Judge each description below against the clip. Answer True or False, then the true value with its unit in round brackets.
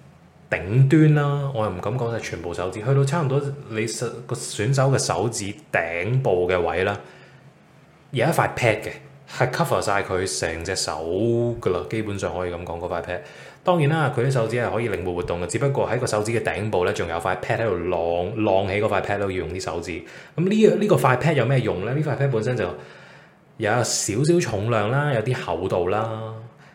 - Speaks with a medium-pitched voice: False (115 Hz)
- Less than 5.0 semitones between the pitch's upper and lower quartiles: False (5.3 semitones)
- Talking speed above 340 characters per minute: False (330 characters per minute)